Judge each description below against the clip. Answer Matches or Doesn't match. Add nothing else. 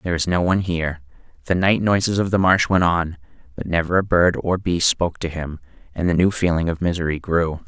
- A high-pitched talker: Doesn't match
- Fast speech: Matches